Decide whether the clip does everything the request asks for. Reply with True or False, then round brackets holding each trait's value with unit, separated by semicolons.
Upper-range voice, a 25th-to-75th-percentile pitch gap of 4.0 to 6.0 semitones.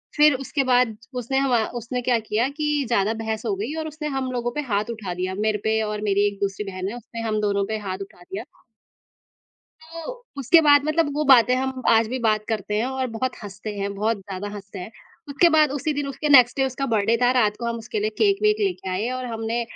True (235 Hz; 4.3 semitones)